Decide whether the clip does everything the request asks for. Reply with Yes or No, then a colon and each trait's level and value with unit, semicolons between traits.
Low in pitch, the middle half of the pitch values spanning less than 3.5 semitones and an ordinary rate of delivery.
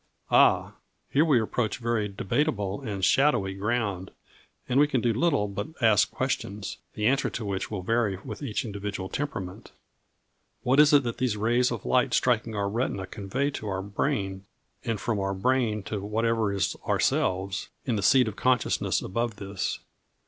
No: low, 110 Hz; average, 4.0 semitones; average, 170 wpm